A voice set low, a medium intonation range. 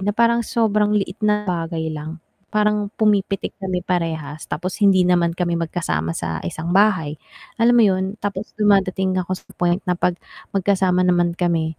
No: medium, 185 Hz; average, 3.3 semitones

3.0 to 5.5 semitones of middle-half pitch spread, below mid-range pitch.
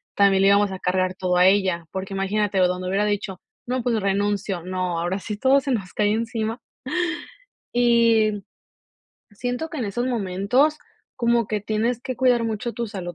No: average, 3.6 semitones; high, 205 Hz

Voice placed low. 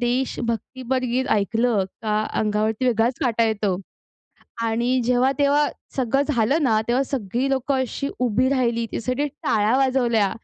No: high, 245 Hz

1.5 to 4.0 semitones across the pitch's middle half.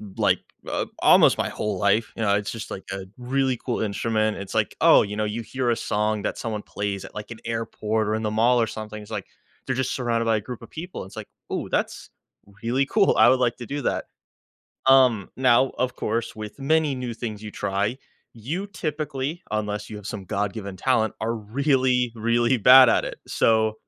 Yes: average, 3.2 semitones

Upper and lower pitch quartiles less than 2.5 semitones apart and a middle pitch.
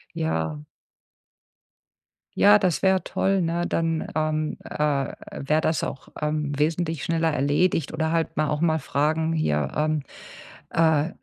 Yes: narrow, 1.9 semitones; medium, 155 Hz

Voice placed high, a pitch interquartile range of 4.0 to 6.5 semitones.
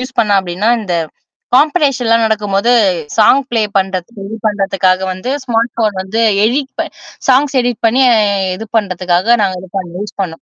Yes: high, 215 Hz; average, 4.3 semitones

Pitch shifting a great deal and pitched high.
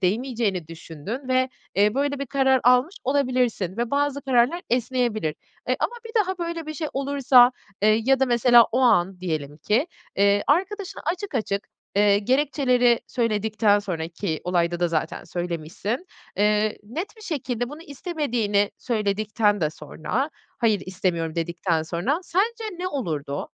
Yes: wide, 6.4 semitones; high, 235 Hz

